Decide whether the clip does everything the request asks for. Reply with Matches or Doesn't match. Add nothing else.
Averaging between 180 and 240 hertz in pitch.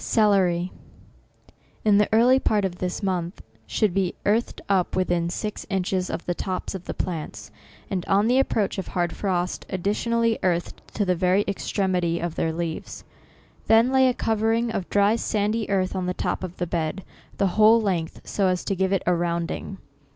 Matches